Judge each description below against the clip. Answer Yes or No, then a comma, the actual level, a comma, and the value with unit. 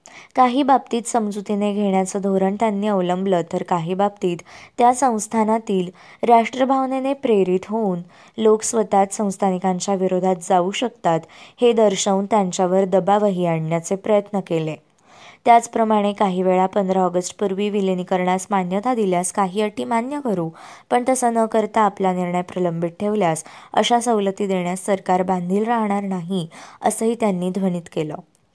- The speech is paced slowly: No, average, 125 wpm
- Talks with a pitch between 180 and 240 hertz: Yes, high, 200 Hz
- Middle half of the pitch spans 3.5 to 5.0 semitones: No, average, 3.1 semitones